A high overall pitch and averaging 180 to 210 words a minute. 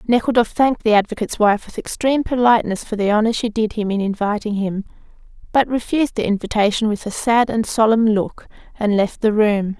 Yes: high, 220 Hz; average, 190 wpm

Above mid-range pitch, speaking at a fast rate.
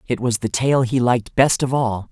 No: low, 120 Hz; fast, 255 wpm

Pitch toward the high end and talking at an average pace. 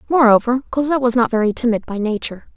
Yes: high, 240 Hz; average, 190 wpm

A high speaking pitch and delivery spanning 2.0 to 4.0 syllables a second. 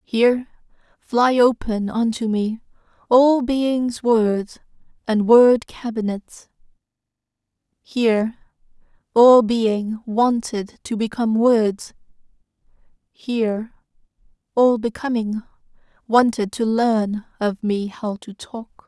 Yes: high, 225 Hz; 3.3 syllables/s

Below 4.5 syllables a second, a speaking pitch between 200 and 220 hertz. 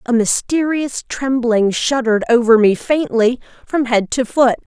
No: 4.3 syllables/s; high, 245 Hz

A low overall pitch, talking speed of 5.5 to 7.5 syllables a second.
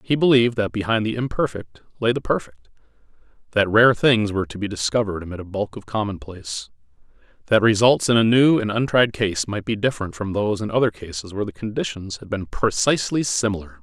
Yes: low, 105 Hz; 6.1 syllables/s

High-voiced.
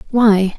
Yes: high, 210 Hz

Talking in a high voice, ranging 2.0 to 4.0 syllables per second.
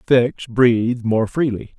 No: low, 120 Hz; 3.8 syllables/s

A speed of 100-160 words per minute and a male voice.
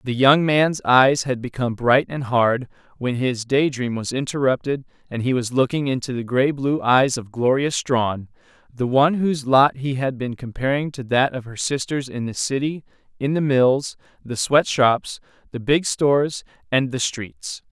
No: average, 180 wpm; male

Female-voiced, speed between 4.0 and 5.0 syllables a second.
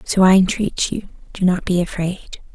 Yes: female; 4.7 syllables/s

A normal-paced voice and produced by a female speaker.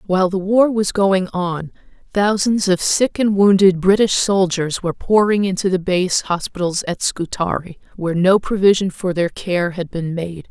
Yes: average, 170 wpm; female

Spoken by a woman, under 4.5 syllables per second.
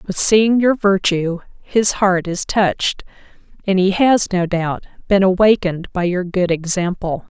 Yes: female; 4.3 syllables/s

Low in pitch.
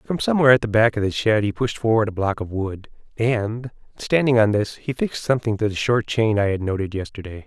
Yes: low, 110 Hz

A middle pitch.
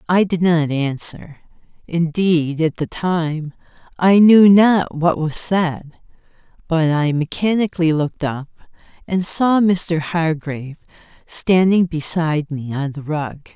Yes: medium, 165 Hz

